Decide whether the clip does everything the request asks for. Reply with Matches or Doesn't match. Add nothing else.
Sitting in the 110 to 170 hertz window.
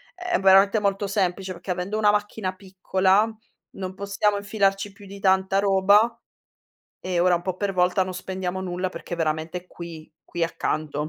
Doesn't match